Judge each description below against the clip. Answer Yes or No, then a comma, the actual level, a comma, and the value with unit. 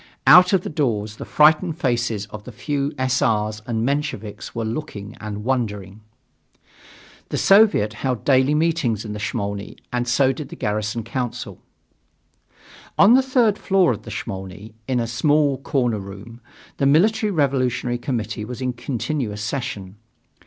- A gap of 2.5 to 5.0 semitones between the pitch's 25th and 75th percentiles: No, wide, 5.4 semitones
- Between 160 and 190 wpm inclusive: No, average, 150 wpm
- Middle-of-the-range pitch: No, low, 125 Hz